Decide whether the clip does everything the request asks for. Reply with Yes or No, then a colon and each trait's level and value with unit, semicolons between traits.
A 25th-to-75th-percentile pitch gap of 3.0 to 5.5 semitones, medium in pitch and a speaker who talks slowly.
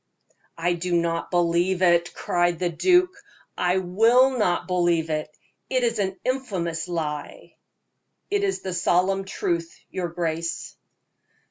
No: narrow, 2.4 semitones; medium, 175 Hz; slow, 130 wpm